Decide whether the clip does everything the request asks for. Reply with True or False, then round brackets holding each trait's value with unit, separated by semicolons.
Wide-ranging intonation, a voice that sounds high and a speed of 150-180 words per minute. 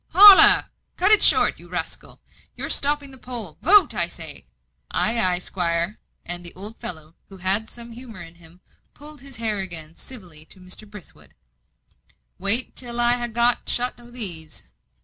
True (5.7 semitones; 215 Hz; 170 wpm)